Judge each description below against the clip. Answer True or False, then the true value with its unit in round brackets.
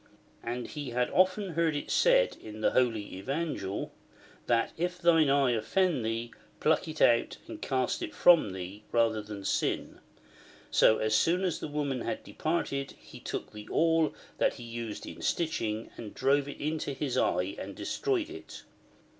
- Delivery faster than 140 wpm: True (170 wpm)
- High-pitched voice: False (135 Hz)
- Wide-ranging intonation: True (6.5 semitones)